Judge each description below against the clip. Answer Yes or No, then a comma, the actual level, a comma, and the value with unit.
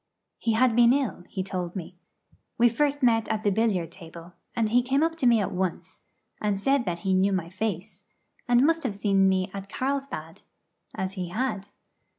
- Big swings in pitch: No, average, 4.6 semitones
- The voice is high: Yes, high, 210 Hz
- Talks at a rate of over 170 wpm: Yes, average, 190 wpm